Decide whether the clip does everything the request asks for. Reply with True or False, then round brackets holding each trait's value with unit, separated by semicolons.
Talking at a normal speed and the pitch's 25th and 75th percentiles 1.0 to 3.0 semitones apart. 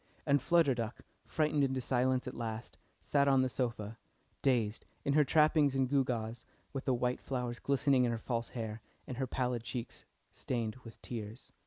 True (175 wpm; 2.7 semitones)